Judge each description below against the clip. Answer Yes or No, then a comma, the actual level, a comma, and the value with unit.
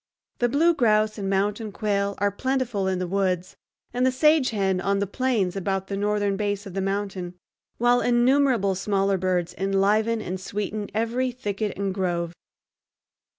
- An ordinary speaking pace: Yes, average, 160 wpm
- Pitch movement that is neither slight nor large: Yes, average, 3.1 semitones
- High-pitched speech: Yes, high, 200 Hz